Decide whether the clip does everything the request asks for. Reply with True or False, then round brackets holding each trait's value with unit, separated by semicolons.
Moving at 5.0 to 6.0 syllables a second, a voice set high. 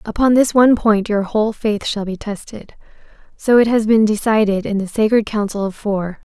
True (5.2 syllables/s; 215 Hz)